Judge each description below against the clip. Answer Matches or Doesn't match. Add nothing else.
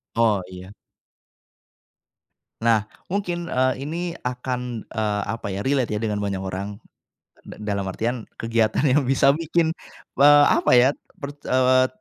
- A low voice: Matches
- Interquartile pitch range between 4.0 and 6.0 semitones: Matches